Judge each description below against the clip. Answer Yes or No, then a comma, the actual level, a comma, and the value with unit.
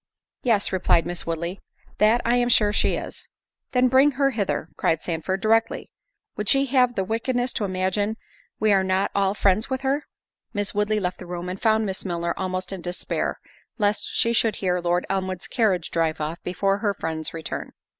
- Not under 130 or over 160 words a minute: No, average, 185 wpm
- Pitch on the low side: No, high, 195 Hz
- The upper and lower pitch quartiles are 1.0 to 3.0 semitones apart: No, average, 3.9 semitones